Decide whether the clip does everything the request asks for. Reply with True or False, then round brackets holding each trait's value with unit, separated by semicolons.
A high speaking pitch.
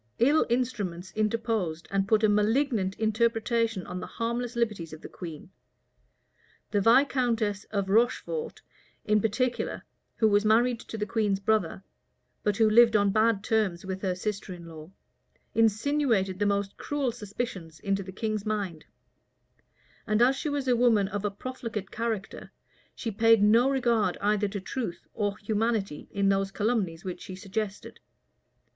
True (215 Hz)